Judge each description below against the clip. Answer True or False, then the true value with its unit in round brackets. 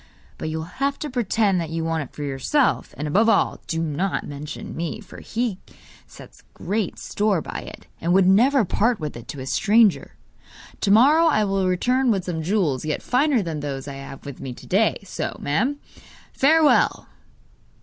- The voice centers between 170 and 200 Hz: True (190 Hz)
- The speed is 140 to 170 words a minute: False (190 wpm)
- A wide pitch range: True (6.8 semitones)